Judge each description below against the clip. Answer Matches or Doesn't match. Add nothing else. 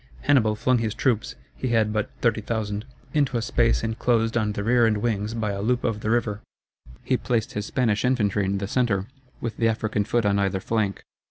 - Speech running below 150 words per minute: Doesn't match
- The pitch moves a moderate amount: Doesn't match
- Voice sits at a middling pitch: Doesn't match